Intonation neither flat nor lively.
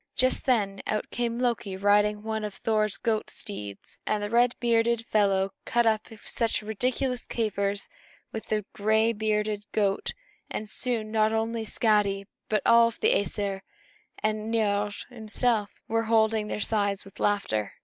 No: narrow, 1.9 semitones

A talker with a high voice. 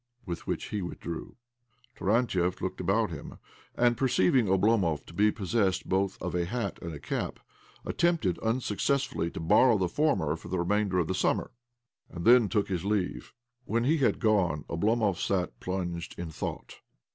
No: very low, 95 Hz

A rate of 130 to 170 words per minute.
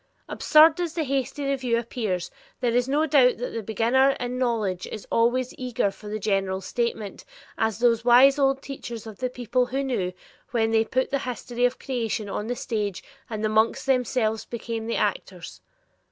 No: average, 180 wpm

